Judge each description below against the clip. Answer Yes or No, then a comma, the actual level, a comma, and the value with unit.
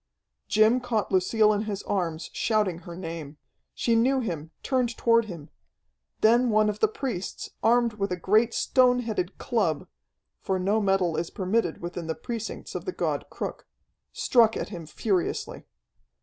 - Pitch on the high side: Yes, high, 210 Hz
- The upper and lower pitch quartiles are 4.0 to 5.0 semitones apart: Yes, average, 4.4 semitones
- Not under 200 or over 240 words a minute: No, average, 160 wpm